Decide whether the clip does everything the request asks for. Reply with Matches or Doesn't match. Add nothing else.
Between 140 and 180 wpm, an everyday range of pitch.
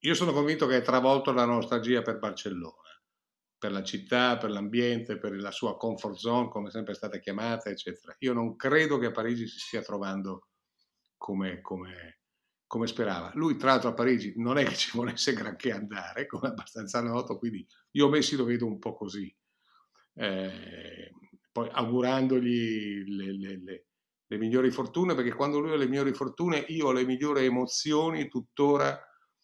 Matches